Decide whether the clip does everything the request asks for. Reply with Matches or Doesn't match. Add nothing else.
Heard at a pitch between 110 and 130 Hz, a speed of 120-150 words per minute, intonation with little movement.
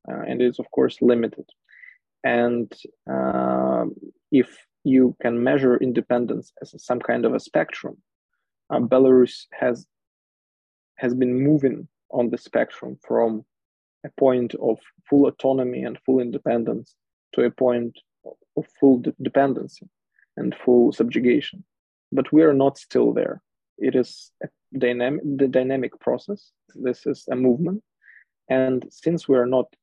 Matches